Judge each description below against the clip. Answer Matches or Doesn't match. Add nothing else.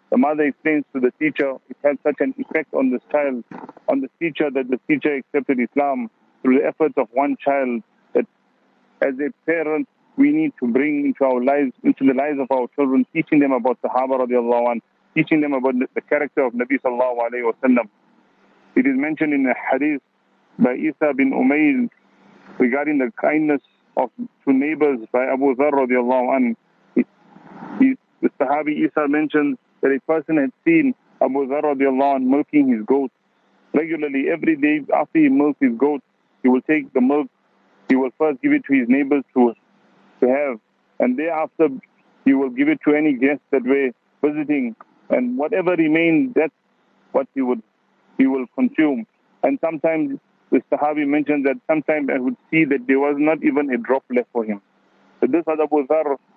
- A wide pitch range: Matches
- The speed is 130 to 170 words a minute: Doesn't match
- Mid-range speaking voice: Matches